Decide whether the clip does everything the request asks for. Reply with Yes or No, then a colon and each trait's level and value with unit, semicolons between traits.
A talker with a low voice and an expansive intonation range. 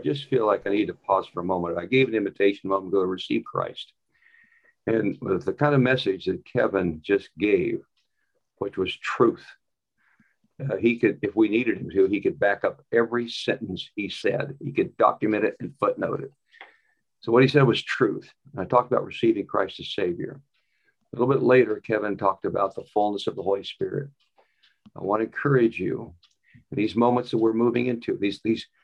Yes: low, 120 Hz; wide, 6.8 semitones